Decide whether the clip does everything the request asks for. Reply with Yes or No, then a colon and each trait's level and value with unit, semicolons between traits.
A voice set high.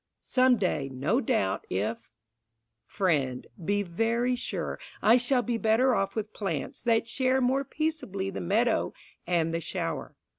Yes: high, 215 Hz